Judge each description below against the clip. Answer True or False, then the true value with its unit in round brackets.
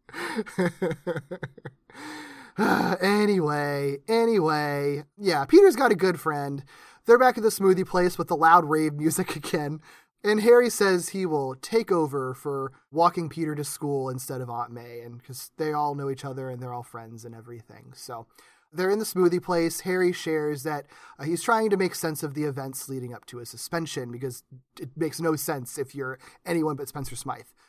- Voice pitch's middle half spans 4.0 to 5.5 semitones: True (5.2 semitones)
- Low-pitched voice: False (155 Hz)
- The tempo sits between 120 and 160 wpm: False (180 wpm)